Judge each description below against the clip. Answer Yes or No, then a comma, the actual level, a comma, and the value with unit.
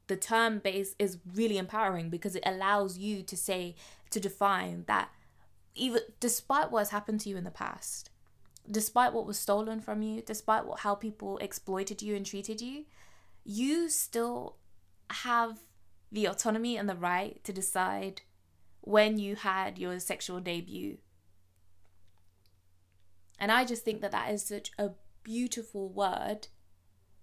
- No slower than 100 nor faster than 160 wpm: Yes, average, 150 wpm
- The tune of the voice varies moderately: Yes, average, 4.0 semitones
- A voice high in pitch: Yes, high, 200 Hz